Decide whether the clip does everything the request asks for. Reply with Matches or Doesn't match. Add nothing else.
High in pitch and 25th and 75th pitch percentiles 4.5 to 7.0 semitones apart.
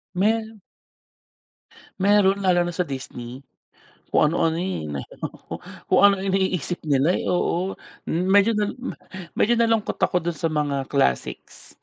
Doesn't match